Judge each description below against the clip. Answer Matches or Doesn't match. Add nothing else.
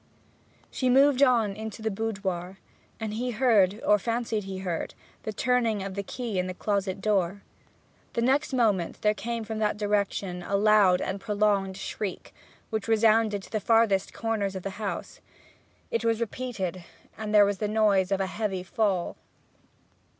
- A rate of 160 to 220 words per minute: Matches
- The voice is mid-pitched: Doesn't match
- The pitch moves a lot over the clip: Doesn't match